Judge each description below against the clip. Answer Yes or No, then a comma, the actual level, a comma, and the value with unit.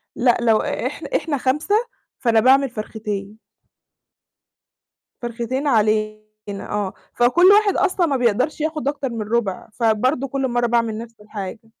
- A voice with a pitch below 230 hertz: No, high, 240 Hz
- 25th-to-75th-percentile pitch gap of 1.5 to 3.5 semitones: No, average, 4.0 semitones